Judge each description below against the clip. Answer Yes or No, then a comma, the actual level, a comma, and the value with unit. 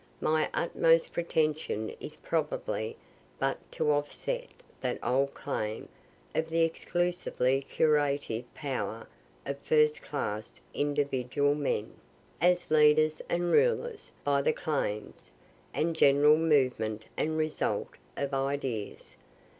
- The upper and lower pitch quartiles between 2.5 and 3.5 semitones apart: Yes, average, 2.8 semitones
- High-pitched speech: No, medium, 145 Hz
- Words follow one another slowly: Yes, slow, 105 wpm